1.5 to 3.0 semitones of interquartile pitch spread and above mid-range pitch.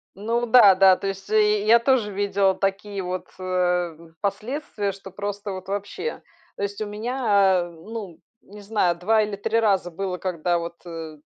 Yes: narrow, 2.5 semitones; high, 200 Hz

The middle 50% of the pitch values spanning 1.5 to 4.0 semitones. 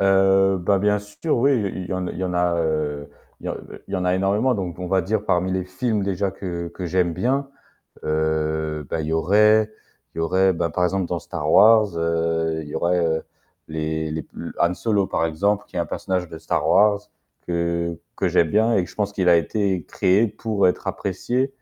Yes: average, 3.4 semitones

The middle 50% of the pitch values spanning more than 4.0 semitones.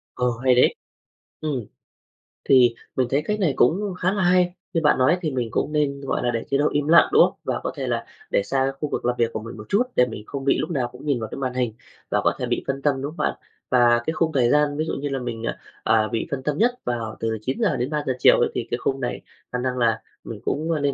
No: average, 3.6 semitones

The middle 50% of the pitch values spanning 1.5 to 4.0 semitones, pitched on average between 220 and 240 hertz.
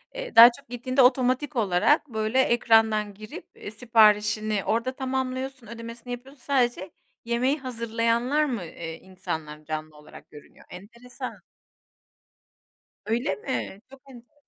Yes: average, 3.5 semitones; high, 235 Hz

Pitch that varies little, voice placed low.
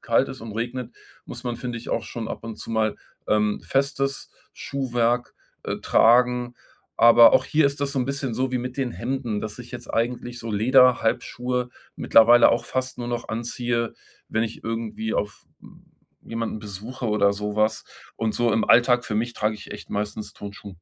Yes: narrow, 2.1 semitones; low, 120 Hz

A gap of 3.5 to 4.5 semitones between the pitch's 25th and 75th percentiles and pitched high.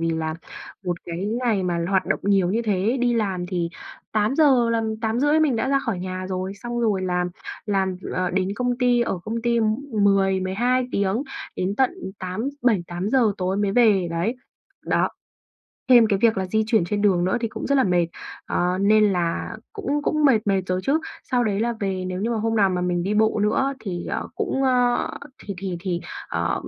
Yes: average, 4.2 semitones; high, 205 Hz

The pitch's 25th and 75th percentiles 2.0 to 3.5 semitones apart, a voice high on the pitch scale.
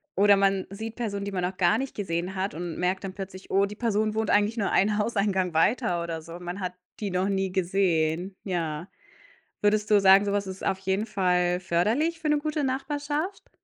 Yes: average, 2.9 semitones; high, 195 Hz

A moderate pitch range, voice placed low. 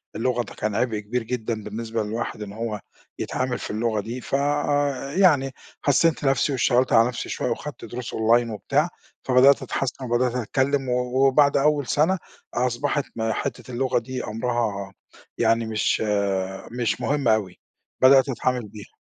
Yes: average, 3.2 semitones; low, 125 Hz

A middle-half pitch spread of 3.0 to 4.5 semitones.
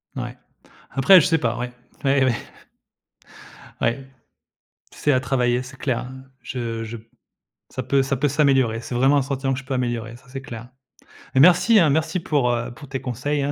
No: narrow, 2.5 semitones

